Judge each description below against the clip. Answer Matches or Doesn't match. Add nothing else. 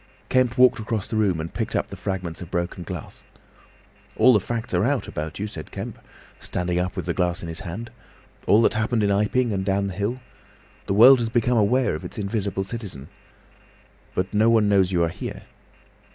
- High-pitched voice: Doesn't match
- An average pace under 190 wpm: Doesn't match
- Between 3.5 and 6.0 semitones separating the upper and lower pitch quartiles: Matches